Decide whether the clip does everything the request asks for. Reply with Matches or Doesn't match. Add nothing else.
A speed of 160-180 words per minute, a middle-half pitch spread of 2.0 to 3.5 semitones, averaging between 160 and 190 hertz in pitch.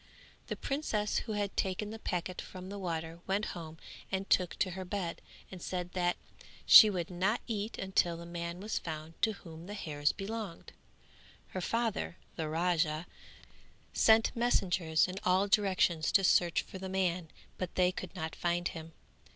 Matches